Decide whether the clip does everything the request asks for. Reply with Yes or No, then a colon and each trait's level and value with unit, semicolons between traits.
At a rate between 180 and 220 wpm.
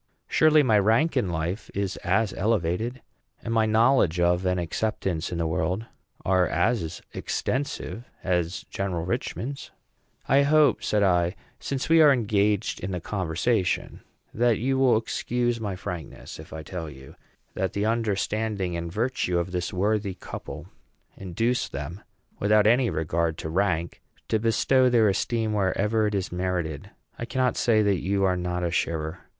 No: average, 155 wpm